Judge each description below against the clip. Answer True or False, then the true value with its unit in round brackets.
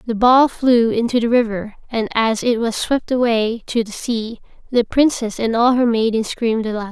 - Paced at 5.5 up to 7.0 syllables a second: False (4.9 syllables/s)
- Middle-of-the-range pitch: False (230 Hz)